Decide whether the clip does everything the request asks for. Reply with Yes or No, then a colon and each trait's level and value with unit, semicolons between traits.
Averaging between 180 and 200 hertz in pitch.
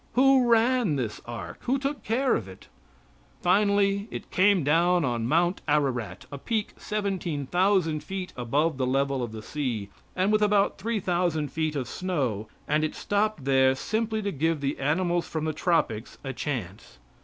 No: medium, 165 Hz